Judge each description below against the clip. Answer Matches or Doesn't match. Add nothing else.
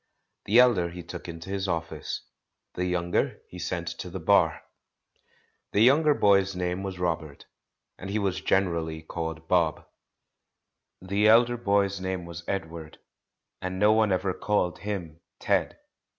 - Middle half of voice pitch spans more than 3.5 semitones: Doesn't match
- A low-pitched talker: Matches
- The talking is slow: Doesn't match